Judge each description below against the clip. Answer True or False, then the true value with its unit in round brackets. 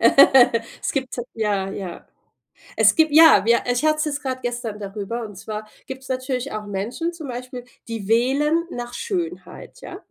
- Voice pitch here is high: True (245 Hz)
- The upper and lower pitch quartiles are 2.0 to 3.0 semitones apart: False (4.7 semitones)